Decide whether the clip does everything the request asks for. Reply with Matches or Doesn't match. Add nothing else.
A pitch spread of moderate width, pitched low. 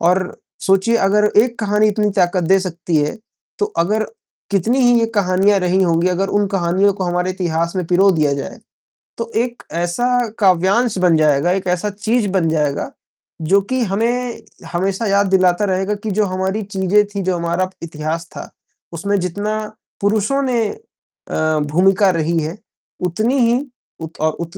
Doesn't match